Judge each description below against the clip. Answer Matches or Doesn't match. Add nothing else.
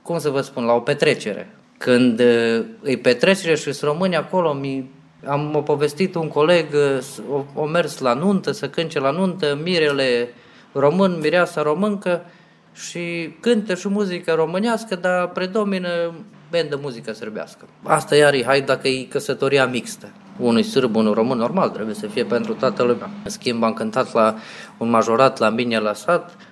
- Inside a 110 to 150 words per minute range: Doesn't match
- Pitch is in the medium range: Matches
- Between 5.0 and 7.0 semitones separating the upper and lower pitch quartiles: Matches